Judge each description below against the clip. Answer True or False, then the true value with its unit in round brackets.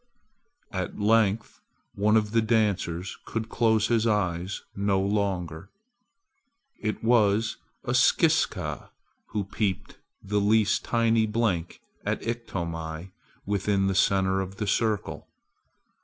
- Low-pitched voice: True (105 Hz)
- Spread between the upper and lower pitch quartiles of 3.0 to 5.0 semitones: False (2.6 semitones)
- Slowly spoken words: True (110 wpm)